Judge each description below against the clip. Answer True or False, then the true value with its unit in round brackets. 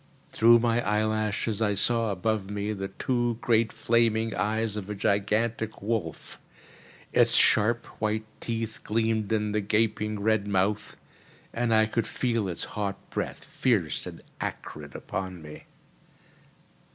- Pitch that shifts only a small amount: True (1.8 semitones)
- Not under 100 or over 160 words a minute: True (135 wpm)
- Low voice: True (110 Hz)